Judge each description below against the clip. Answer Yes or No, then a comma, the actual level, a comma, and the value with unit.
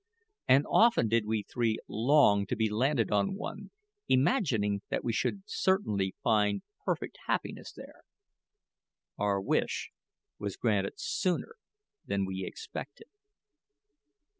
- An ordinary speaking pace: No, slow, 115 wpm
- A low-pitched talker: Yes, low, 110 Hz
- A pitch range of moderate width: No, wide, 6.3 semitones